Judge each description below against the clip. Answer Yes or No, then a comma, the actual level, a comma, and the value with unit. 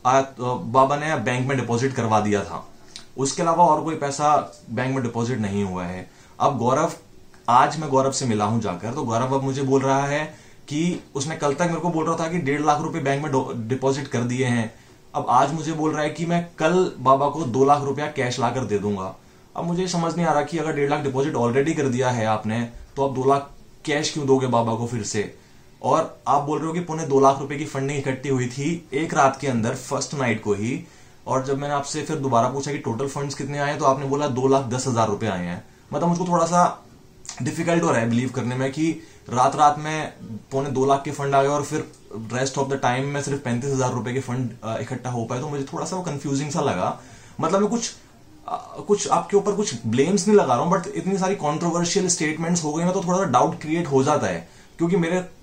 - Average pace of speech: No, fast, 235 wpm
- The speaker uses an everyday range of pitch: Yes, average, 3.7 semitones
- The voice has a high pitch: No, medium, 140 Hz